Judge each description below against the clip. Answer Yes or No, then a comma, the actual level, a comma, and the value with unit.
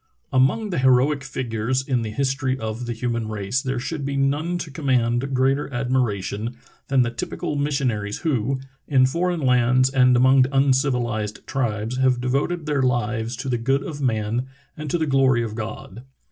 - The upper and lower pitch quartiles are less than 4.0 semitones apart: Yes, narrow, 2.6 semitones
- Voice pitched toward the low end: Yes, low, 130 Hz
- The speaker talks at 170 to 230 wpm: Yes, average, 180 wpm